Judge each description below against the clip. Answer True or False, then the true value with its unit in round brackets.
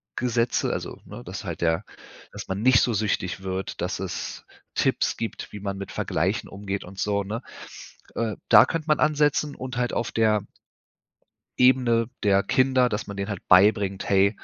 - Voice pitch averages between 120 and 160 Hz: False (105 Hz)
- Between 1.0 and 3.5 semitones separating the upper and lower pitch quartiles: False (3.9 semitones)